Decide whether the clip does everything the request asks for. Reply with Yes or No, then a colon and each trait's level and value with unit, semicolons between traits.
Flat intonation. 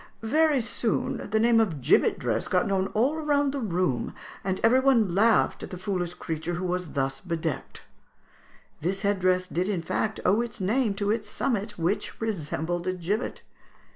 No: average, 4.2 semitones